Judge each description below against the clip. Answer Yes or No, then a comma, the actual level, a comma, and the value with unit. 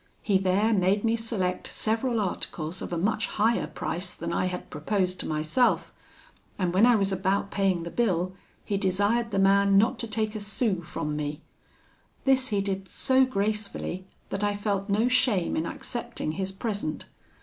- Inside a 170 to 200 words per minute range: Yes, average, 175 wpm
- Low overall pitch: No, high, 200 Hz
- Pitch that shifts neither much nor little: Yes, average, 3.2 semitones